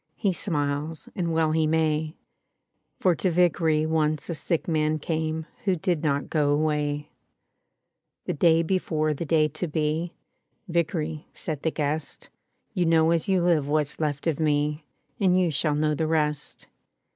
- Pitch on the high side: No, medium, 155 Hz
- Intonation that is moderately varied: No, narrow, 1.8 semitones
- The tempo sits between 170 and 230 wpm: No, average, 155 wpm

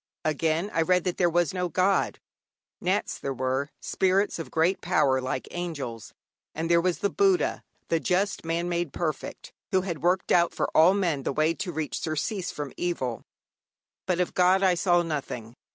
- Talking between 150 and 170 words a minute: No, average, 180 wpm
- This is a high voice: No, medium, 170 Hz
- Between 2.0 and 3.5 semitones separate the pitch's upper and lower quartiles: Yes, average, 2.9 semitones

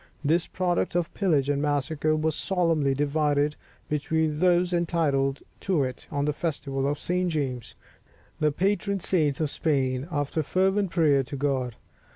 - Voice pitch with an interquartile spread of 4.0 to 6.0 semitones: No, average, 3.5 semitones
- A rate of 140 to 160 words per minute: Yes, average, 150 wpm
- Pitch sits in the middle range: Yes, medium, 150 Hz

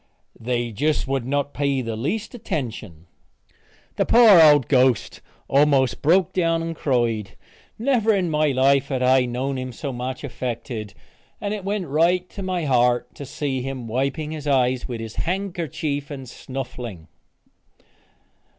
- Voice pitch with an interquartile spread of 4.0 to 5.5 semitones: Yes, average, 4.6 semitones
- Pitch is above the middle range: No, low, 135 Hz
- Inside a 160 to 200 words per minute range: No, average, 145 wpm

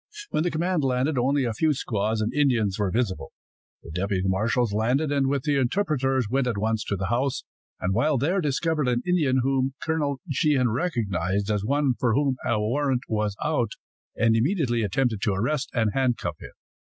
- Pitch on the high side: No, low, 125 Hz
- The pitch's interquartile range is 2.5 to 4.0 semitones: No, average, 4.7 semitones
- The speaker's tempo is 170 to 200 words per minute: Yes, average, 185 wpm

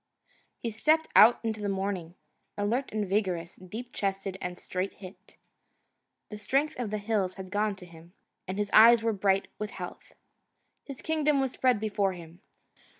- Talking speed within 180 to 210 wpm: No, average, 165 wpm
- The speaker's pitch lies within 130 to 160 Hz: No, high, 205 Hz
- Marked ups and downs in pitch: No, average, 3.2 semitones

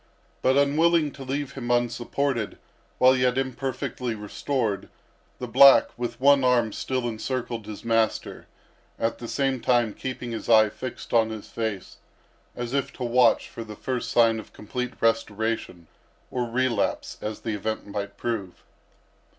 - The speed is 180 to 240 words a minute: No, average, 150 wpm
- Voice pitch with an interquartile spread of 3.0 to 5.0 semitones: No, narrow, 2.6 semitones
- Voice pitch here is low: Yes, low, 120 Hz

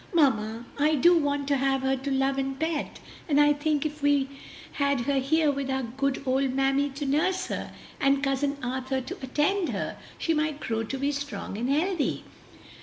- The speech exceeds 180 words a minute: Yes, average, 190 wpm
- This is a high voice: Yes, very high, 280 Hz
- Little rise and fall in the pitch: Yes, narrow, 1.8 semitones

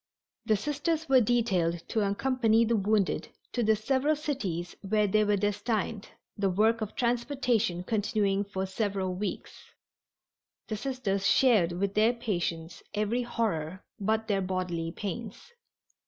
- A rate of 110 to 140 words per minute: Yes, slow, 135 wpm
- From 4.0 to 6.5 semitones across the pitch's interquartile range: No, average, 3.6 semitones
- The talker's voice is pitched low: No, high, 210 Hz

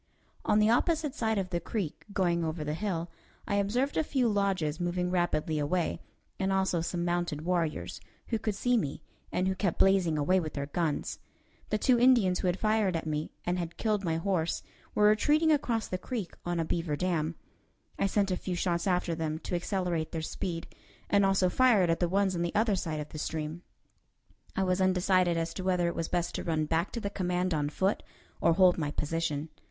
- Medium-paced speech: No, fast, 210 wpm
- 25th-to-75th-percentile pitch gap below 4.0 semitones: Yes, average, 3.3 semitones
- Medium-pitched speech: Yes, medium, 180 Hz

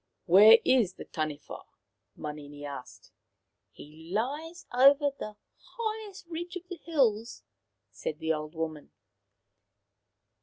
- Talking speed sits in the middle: No, slow, 125 wpm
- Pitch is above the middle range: Yes, high, 220 Hz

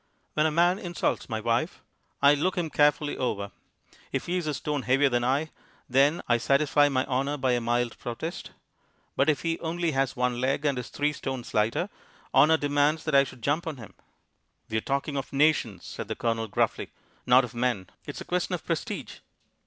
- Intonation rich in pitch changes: No, average, 3.7 semitones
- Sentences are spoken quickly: No, average, 195 wpm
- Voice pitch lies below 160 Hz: Yes, medium, 140 Hz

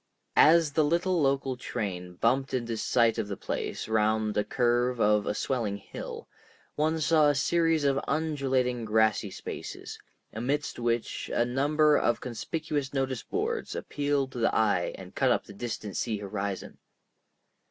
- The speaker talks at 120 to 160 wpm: Yes, average, 155 wpm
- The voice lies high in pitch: No, low, 125 Hz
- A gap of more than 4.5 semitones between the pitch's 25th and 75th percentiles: Yes, average, 4.9 semitones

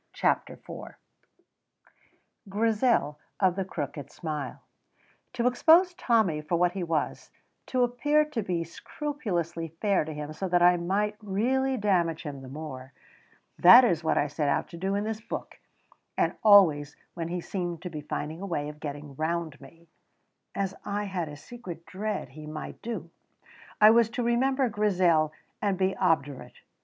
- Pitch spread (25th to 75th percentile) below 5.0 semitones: No, wide, 5.5 semitones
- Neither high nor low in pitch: Yes, medium, 180 Hz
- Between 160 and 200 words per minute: Yes, average, 165 wpm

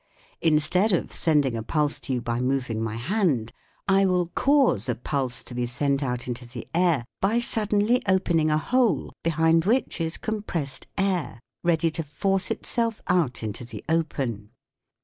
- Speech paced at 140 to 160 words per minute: No, average, 175 wpm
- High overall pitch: No, medium, 155 Hz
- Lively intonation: Yes, wide, 7.2 semitones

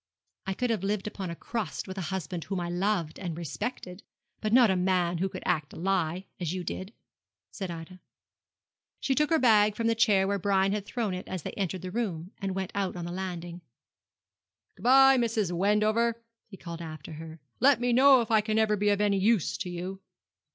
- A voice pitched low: No, high, 195 Hz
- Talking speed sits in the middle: No, fast, 215 wpm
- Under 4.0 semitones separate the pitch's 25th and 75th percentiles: Yes, average, 3.3 semitones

